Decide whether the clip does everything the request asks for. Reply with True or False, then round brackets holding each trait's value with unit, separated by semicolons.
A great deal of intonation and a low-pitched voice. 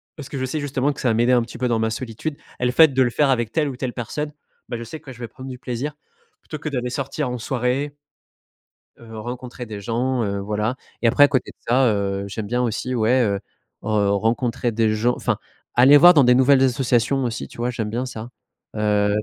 False (2.8 semitones; 125 Hz)